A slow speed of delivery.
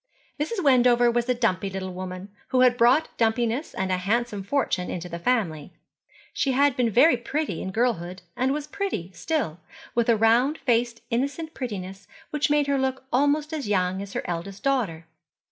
No: average, 180 wpm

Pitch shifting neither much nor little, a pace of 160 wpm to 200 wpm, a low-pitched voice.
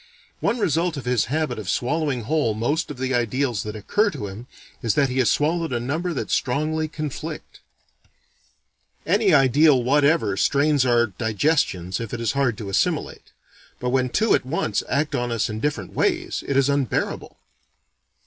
Yes: average, 4.7 semitones; average, 170 wpm; low, 130 Hz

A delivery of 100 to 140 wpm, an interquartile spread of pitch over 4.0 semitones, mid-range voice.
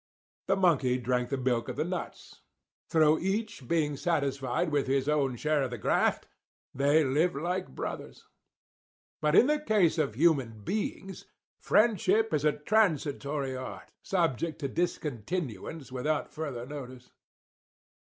Yes: slow, 135 wpm; average, 4.7 semitones; medium, 150 Hz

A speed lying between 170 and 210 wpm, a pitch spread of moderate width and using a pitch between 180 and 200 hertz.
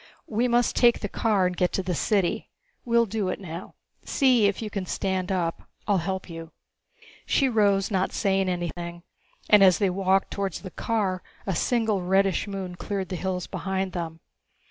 No: average, 180 wpm; narrow, 2.3 semitones; high, 190 Hz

